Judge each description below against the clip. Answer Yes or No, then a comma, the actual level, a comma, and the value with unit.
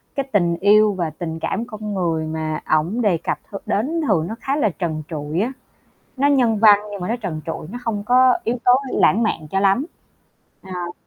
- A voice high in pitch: Yes, high, 200 Hz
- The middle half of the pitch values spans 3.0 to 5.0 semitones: No, wide, 5.5 semitones